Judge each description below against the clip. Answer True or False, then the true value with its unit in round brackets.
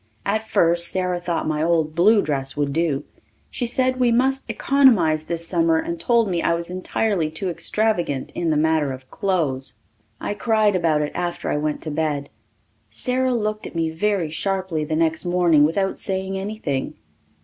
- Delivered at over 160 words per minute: True (175 wpm)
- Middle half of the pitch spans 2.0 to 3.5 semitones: False (4.8 semitones)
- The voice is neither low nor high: True (170 Hz)